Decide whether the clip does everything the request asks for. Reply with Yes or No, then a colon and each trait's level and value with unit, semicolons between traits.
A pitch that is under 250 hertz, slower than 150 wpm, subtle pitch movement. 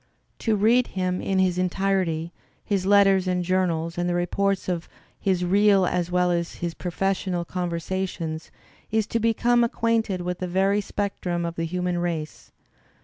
No: medium, 185 Hz; average, 170 wpm; narrow, 2.1 semitones